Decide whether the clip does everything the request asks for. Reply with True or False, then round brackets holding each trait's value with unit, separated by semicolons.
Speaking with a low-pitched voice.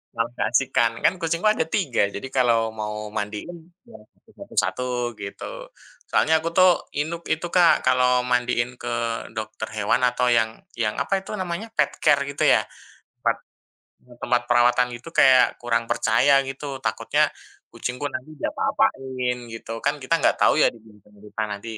True (125 Hz)